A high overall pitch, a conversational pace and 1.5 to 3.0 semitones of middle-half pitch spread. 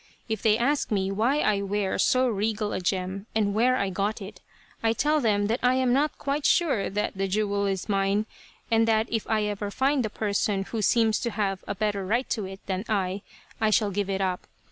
No: high, 210 Hz; fast, 220 wpm; narrow, 2.5 semitones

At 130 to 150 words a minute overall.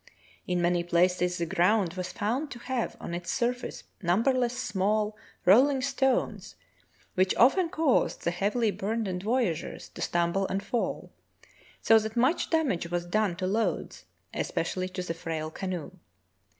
Yes: average, 145 wpm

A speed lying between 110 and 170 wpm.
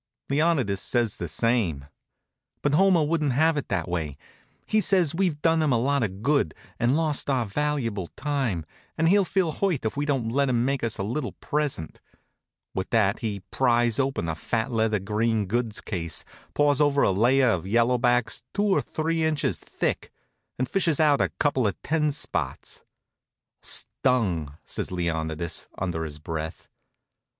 Yes: average, 165 wpm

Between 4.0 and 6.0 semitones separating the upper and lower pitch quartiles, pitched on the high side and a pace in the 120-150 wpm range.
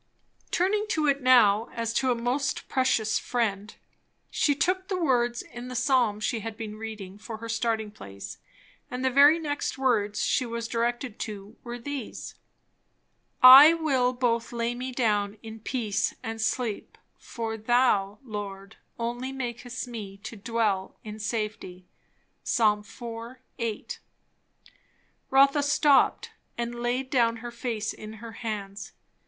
No: average, 3.0 semitones; high, 235 Hz; average, 145 wpm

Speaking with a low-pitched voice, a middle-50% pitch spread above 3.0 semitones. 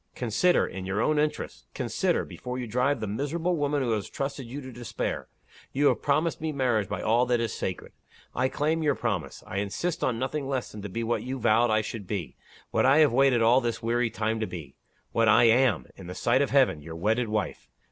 Yes: low, 120 Hz; average, 4.2 semitones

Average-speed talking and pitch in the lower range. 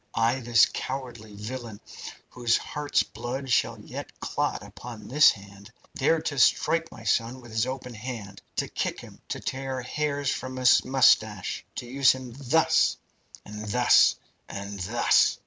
Yes: average, 150 wpm; low, 125 Hz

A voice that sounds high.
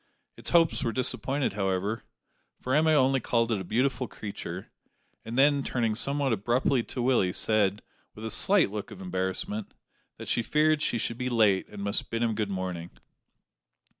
No: low, 115 Hz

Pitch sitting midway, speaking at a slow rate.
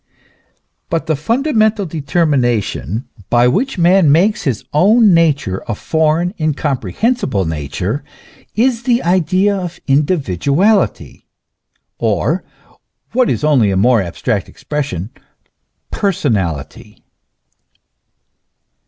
Yes: medium, 155 Hz; slow, 95 wpm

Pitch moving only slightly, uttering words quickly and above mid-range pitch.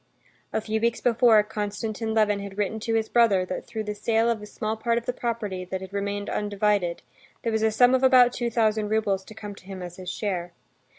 Yes: narrow, 2.1 semitones; fast, 230 wpm; high, 215 Hz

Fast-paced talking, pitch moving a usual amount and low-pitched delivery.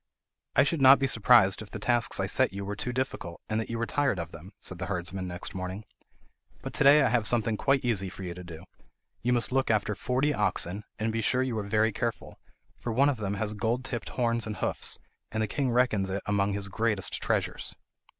Yes: fast, 230 wpm; average, 3.9 semitones; low, 110 Hz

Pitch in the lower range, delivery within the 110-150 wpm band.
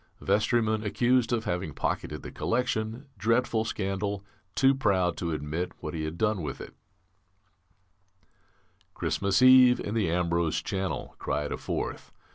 Yes: low, 100 Hz; average, 140 wpm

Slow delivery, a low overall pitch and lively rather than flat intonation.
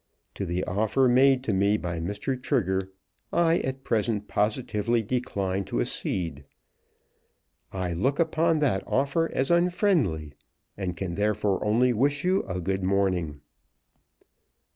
Yes: slow, 130 wpm; low, 105 Hz; wide, 6.0 semitones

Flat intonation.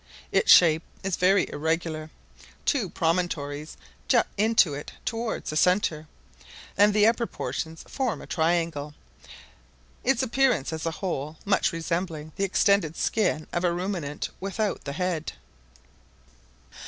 No: average, 4.3 semitones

